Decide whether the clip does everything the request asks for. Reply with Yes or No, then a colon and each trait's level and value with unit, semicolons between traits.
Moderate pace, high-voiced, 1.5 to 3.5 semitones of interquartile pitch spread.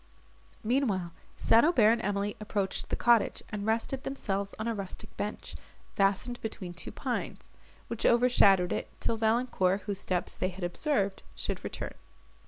Yes: average, 150 wpm; high, 210 Hz; average, 3.2 semitones